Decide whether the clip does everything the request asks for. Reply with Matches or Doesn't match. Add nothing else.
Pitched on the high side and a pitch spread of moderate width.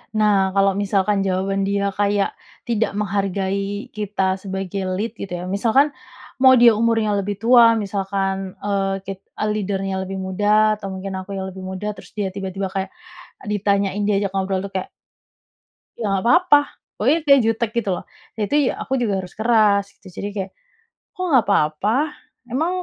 Doesn't match